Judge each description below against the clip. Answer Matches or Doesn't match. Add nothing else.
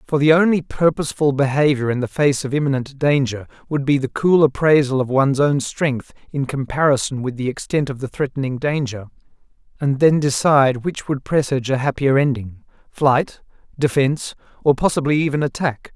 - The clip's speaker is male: Matches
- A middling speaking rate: Matches